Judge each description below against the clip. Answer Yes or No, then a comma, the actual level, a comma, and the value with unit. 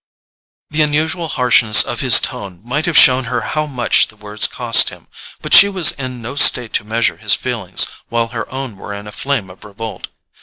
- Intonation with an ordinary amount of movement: Yes, average, 4.7 semitones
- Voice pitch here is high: No, low, 120 Hz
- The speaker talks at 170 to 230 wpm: Yes, average, 200 wpm